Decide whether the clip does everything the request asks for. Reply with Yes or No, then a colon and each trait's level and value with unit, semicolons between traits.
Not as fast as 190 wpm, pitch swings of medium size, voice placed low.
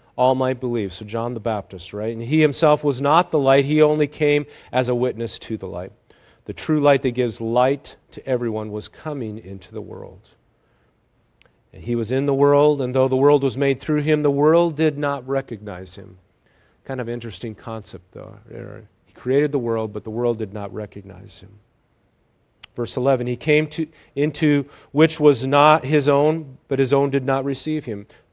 No: average, 195 wpm; average, 4.5 semitones; low, 130 Hz